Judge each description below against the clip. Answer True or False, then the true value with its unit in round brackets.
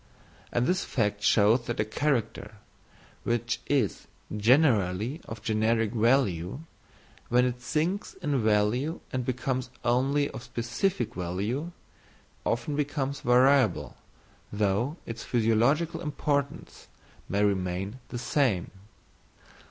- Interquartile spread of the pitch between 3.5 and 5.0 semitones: True (4.6 semitones)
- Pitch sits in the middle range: False (120 Hz)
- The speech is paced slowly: True (105 wpm)